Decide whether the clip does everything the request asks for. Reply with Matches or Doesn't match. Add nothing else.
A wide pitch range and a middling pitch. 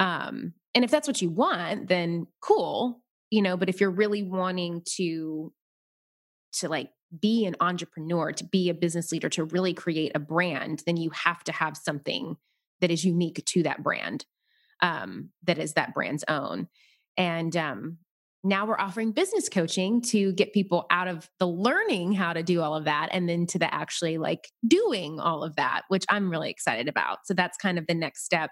Doesn't match